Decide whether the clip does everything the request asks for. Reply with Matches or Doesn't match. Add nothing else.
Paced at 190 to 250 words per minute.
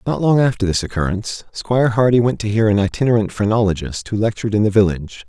Matches